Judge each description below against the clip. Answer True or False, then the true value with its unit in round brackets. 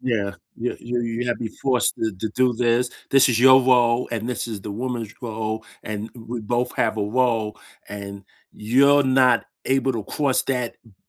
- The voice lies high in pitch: False (120 Hz)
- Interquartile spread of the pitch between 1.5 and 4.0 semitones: True (2.4 semitones)